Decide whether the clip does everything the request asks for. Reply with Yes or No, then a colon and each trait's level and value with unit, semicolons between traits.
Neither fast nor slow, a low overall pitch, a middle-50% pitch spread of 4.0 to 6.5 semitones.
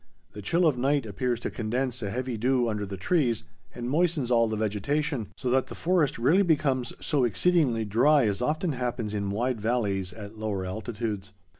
Yes: average, 185 wpm; low, 120 Hz; average, 4.4 semitones